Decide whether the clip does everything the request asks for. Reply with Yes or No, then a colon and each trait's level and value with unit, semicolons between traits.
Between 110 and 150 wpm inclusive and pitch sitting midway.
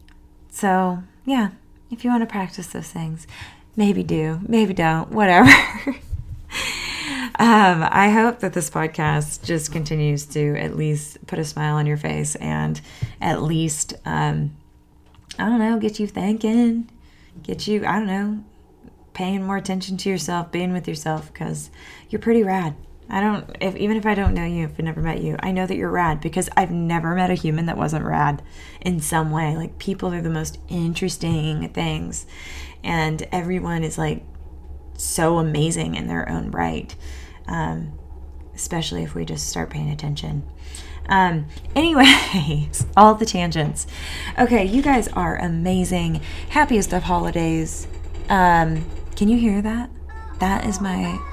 No: average, 160 wpm; medium, 165 Hz